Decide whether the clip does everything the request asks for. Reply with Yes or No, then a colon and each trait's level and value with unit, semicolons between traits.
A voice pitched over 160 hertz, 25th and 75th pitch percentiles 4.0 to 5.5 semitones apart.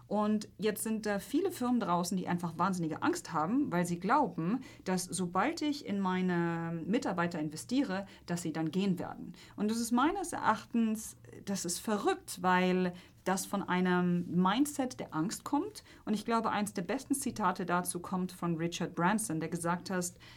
Yes: high, 190 Hz; average, 4.7 semitones